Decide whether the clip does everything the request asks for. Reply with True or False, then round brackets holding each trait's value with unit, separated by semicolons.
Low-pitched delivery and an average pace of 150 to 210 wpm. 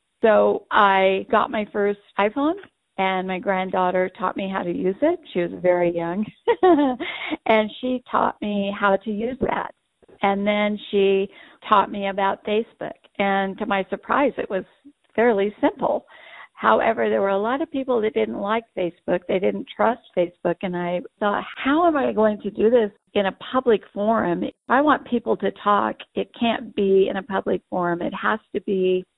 False (205 Hz; 180 wpm)